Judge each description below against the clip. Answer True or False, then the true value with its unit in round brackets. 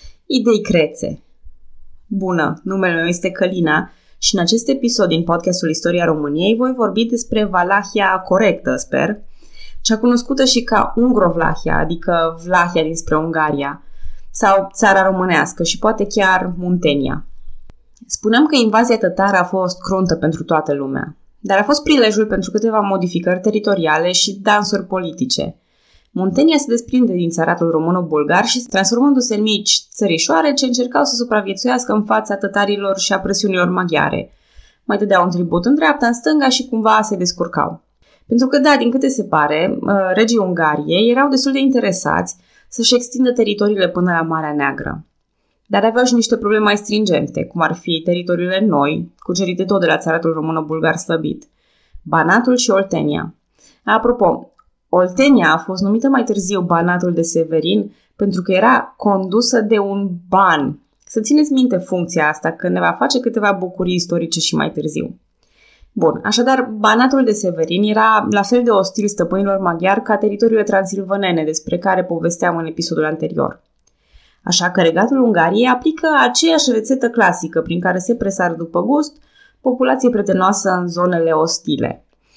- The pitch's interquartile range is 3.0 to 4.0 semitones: False (4.9 semitones)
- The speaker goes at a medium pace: True (150 wpm)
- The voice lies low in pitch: False (195 Hz)